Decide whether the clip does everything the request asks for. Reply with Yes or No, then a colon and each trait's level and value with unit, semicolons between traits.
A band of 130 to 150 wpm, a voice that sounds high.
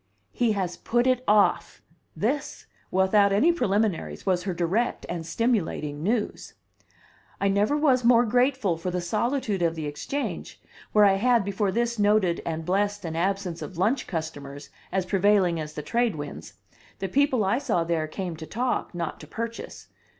No: average, 165 wpm; high, 200 Hz